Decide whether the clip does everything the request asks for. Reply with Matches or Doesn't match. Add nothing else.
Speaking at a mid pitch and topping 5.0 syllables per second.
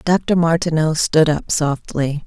Doesn't match